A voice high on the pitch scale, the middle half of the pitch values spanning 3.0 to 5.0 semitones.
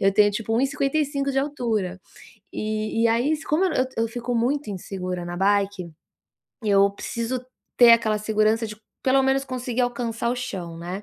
Yes: high, 230 Hz; average, 4.2 semitones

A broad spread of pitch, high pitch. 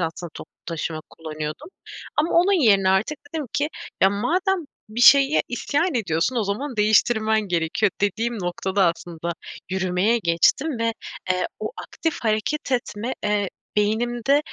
Yes: wide, 6.2 semitones; high, 215 Hz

